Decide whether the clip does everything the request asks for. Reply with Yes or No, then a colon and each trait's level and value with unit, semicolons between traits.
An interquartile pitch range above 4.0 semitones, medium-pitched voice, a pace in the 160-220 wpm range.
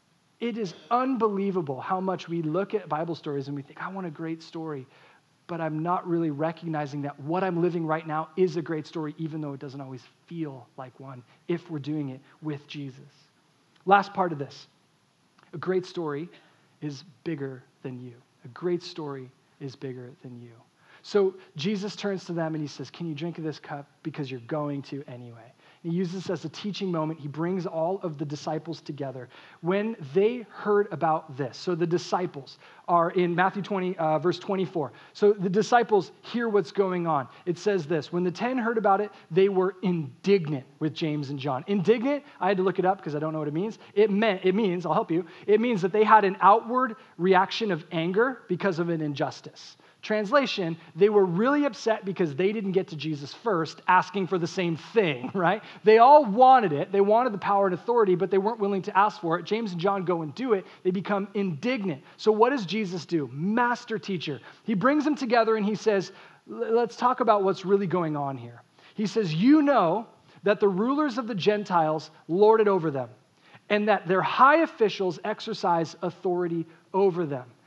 Yes: average, 4.6 semitones; medium, 180 Hz; average, 200 wpm